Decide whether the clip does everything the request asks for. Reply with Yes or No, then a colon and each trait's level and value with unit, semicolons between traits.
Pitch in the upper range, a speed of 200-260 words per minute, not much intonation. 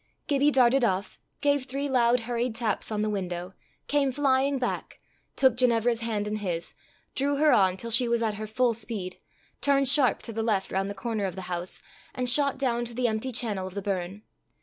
No: high, 235 Hz; fast, 205 wpm; average, 4.2 semitones